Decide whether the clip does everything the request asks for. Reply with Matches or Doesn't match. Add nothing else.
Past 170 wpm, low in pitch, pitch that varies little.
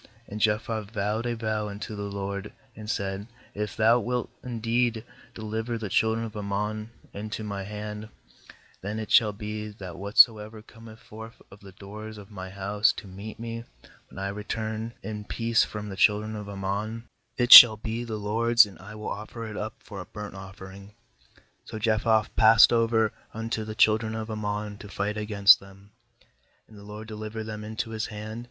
Matches